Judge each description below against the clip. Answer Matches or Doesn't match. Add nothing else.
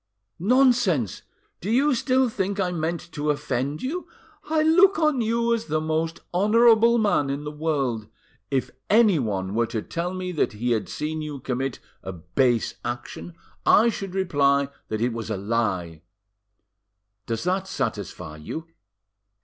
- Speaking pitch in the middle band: Matches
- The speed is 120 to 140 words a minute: Doesn't match